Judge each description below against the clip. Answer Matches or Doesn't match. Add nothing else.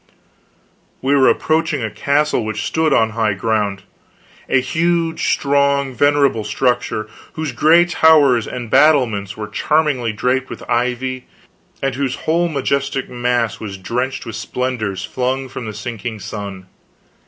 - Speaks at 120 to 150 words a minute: Matches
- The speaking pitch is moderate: Doesn't match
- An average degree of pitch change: Matches